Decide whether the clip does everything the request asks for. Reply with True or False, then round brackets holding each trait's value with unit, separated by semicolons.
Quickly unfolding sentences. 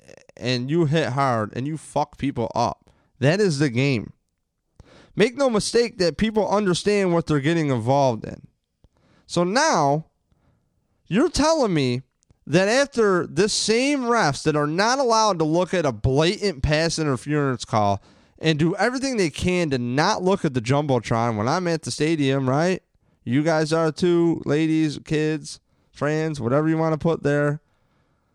False (160 wpm)